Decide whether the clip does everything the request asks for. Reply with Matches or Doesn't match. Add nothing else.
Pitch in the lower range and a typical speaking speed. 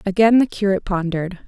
Doesn't match